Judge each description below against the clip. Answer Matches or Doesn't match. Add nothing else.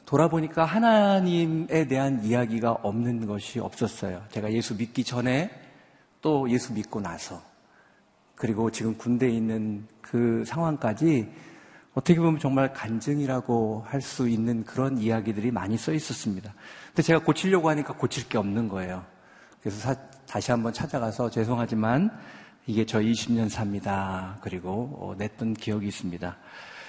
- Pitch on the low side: Matches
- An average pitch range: Matches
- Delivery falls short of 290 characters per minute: Doesn't match